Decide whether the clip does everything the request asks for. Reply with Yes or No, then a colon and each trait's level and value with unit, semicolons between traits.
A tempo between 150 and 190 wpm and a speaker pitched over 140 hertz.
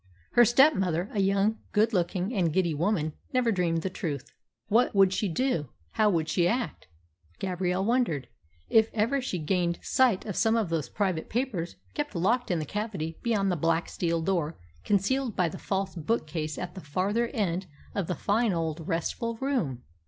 Yes: average, 175 wpm; high, 190 Hz